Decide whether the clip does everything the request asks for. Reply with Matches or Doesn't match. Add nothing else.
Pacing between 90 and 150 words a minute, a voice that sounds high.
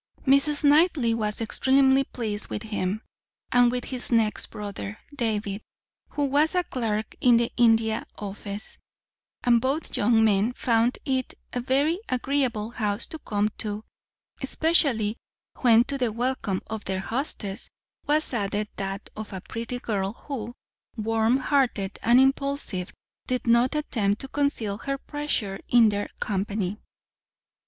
Matches